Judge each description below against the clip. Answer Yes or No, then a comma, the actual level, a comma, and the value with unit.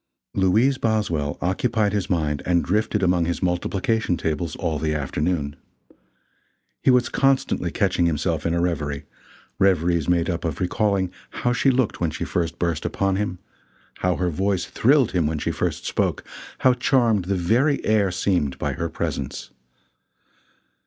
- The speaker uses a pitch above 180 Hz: No, very low, 90 Hz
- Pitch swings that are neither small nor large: Yes, average, 4.2 semitones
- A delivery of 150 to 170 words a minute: Yes, average, 155 wpm